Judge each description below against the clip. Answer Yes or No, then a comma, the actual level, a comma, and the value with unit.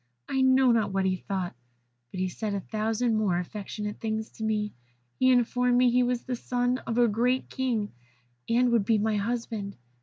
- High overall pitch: Yes, high, 225 Hz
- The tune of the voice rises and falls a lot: No, average, 2.9 semitones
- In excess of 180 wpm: Yes, average, 190 wpm